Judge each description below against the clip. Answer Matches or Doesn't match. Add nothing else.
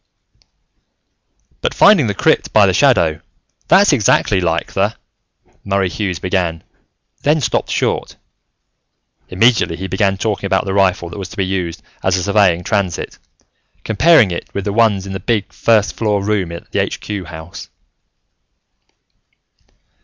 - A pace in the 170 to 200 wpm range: Doesn't match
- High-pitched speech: Doesn't match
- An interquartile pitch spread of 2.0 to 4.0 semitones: Matches